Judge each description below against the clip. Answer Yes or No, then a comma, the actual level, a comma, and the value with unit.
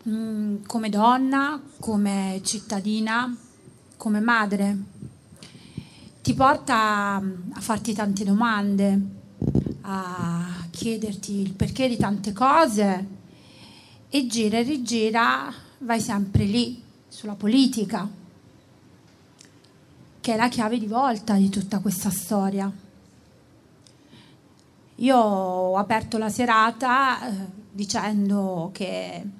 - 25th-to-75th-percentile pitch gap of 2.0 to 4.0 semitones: Yes, average, 2.8 semitones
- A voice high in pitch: Yes, high, 215 Hz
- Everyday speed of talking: No, slow, 100 wpm